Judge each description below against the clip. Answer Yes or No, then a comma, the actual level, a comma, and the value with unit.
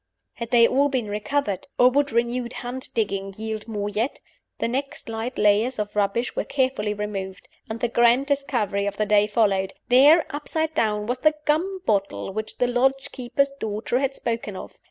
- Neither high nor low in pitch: No, high, 235 Hz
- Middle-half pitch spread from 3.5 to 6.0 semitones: Yes, average, 4.1 semitones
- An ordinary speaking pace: Yes, average, 180 wpm